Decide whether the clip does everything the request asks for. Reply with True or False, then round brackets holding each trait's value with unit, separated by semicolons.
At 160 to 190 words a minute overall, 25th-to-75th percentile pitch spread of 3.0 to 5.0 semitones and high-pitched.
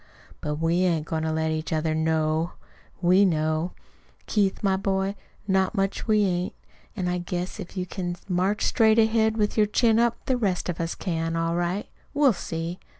False (185 wpm; 3.8 semitones; 180 Hz)